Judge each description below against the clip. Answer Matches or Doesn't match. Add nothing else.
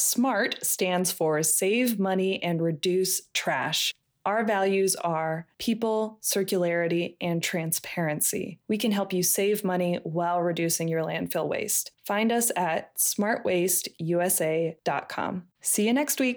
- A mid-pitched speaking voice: Matches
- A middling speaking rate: Doesn't match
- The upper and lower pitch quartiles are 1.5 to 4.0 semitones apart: Matches